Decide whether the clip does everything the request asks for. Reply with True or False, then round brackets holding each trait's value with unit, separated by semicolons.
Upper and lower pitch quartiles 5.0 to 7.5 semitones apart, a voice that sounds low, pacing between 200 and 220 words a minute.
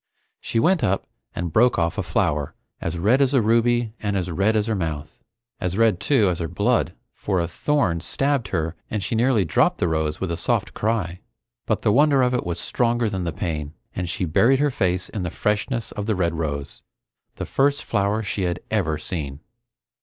True (5.5 semitones; 100 Hz; 205 wpm)